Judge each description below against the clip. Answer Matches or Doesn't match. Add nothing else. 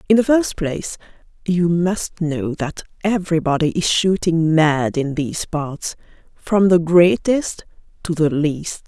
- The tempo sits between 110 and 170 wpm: Matches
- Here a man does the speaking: Doesn't match